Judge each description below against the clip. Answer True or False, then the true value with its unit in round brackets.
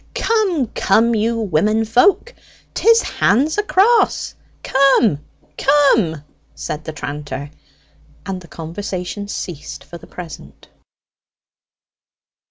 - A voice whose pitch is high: True (210 Hz)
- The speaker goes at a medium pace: False (95 wpm)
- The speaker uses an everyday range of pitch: False (8.8 semitones)